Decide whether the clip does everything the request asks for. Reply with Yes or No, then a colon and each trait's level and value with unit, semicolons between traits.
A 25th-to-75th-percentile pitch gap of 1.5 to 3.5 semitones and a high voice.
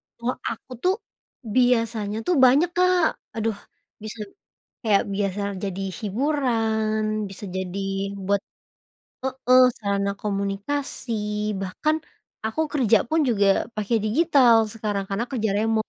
No: average, 4.0 semitones; high, 225 Hz